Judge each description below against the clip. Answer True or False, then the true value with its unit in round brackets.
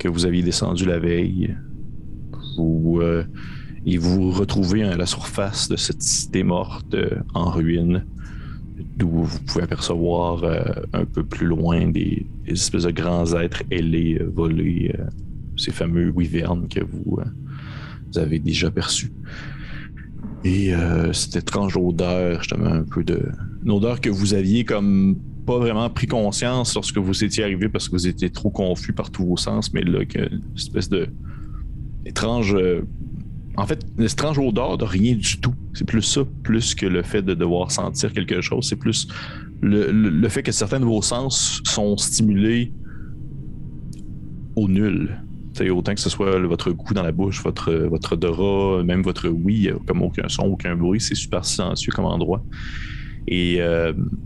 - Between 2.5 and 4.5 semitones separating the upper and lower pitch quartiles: True (3.8 semitones)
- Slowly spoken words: False (165 wpm)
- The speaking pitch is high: False (95 Hz)